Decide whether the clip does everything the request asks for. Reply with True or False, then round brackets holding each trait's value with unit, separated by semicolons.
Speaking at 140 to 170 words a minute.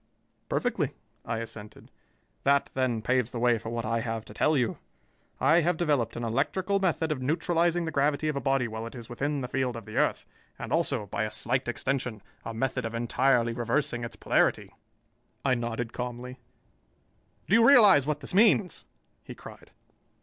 False (180 wpm)